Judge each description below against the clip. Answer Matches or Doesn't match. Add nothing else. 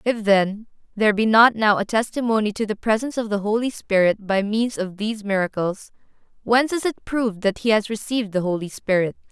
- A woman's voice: Matches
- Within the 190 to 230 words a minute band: Matches